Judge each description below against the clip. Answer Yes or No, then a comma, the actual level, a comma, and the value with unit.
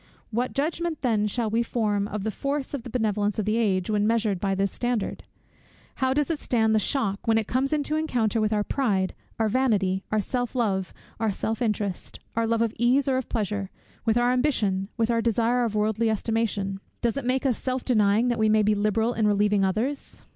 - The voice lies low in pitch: No, high, 225 Hz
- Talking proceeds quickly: Yes, fast, 210 wpm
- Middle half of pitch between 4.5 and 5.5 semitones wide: No, average, 3.0 semitones